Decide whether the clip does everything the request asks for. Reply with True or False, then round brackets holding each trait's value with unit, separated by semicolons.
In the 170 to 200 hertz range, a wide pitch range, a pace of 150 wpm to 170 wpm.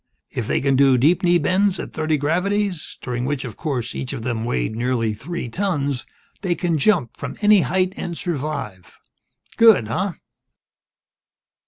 False (150 Hz; 6.5 semitones; 160 wpm)